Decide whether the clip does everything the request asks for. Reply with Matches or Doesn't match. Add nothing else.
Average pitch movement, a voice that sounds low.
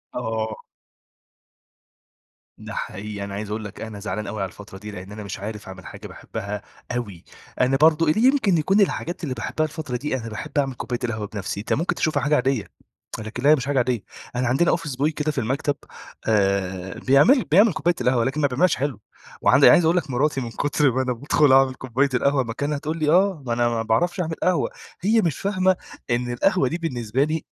Doesn't match